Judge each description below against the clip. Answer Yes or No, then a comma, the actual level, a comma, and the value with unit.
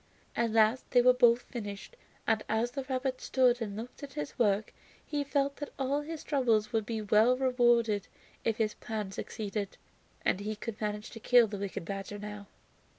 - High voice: Yes, high, 225 Hz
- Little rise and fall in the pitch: No, average, 3.3 semitones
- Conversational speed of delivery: Yes, average, 185 wpm